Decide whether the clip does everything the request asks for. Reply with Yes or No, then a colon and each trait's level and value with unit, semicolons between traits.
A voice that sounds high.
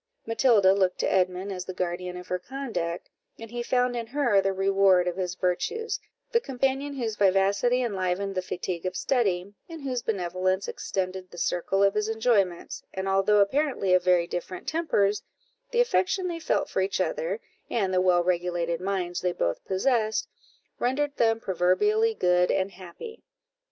Yes: high, 195 Hz